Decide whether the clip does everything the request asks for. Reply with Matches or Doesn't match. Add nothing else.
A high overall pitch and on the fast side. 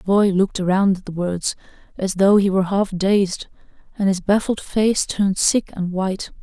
Doesn't match